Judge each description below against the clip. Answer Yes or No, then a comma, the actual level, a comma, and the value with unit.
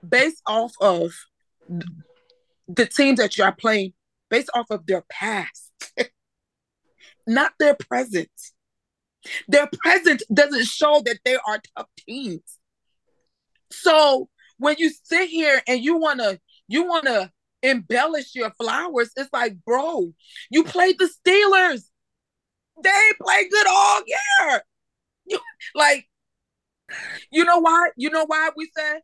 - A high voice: Yes, very high, 290 Hz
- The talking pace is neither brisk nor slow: No, slow, 125 wpm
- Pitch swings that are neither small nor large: No, wide, 6.6 semitones